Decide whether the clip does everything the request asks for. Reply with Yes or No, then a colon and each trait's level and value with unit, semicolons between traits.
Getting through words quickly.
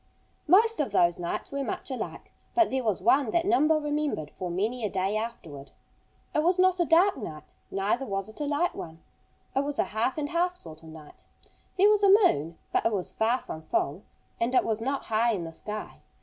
Yes: fast, 215 wpm